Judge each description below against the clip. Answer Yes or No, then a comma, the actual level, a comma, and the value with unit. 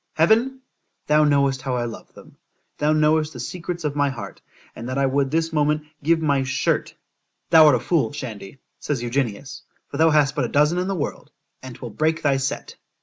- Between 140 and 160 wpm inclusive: No, average, 190 wpm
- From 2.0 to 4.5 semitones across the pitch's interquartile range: Yes, average, 3.0 semitones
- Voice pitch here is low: No, medium, 145 Hz